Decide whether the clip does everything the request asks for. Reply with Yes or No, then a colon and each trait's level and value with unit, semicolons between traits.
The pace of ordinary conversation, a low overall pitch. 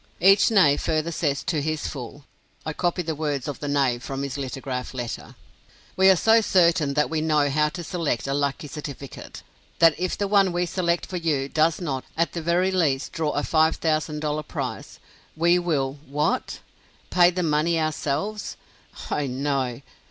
No: average, 175 wpm; medium, 155 Hz